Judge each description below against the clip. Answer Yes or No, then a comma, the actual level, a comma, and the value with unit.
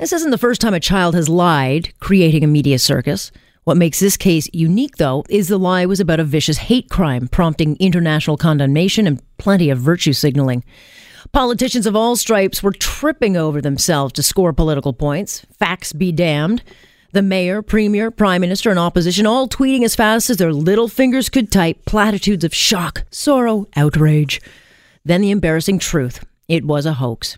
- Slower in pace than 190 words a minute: Yes, average, 180 wpm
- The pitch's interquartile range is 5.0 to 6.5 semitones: Yes, wide, 5.4 semitones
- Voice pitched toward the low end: No, medium, 175 Hz